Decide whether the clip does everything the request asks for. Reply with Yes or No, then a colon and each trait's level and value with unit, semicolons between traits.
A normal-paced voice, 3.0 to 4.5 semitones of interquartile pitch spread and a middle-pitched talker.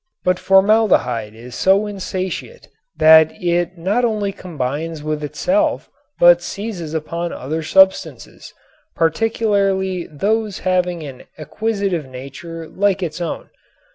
No: slow, 110 wpm; average, 4.1 semitones; medium, 180 Hz